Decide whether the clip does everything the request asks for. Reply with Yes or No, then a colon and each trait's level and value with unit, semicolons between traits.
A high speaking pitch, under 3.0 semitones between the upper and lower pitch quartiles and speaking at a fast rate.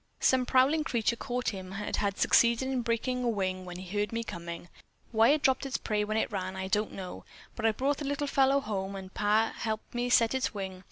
No: high, 225 Hz; average, 4.7 semitones; fast, 230 wpm